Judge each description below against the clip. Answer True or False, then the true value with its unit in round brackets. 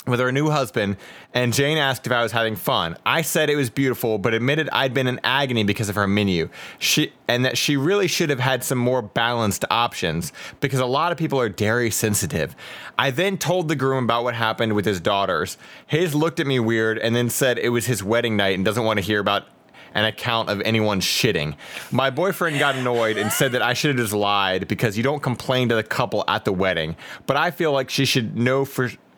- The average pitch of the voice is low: True (120 Hz)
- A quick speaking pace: True (230 wpm)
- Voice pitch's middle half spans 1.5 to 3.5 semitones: False (3.9 semitones)